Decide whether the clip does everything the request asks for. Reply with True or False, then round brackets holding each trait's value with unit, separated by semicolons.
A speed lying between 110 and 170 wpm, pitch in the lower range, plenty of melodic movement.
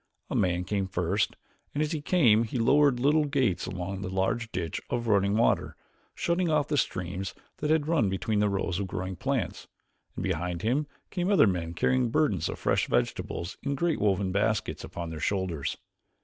False (185 wpm; 105 Hz; 7.3 semitones)